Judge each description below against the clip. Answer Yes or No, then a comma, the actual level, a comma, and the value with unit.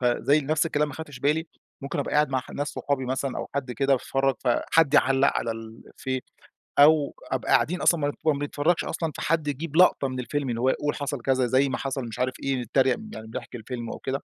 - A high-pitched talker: No, low, 135 Hz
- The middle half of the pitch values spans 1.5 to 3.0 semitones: Yes, narrow, 2.5 semitones